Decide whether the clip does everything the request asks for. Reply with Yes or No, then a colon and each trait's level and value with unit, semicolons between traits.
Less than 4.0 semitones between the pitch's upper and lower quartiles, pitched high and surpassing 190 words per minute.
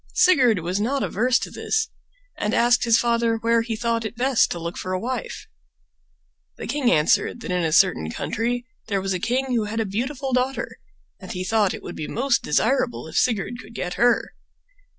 No: average, 4.3 semitones; high, 230 Hz; average, 200 wpm